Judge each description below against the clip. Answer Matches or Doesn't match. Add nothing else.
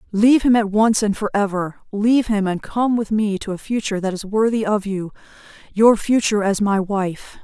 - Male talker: Doesn't match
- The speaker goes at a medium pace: Matches